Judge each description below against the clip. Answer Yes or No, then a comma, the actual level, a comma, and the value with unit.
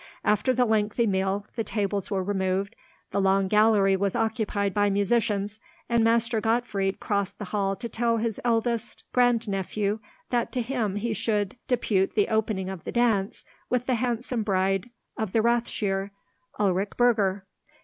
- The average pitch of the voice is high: Yes, high, 210 Hz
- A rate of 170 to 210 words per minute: No, average, 155 wpm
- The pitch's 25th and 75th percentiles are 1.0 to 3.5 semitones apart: Yes, average, 2.9 semitones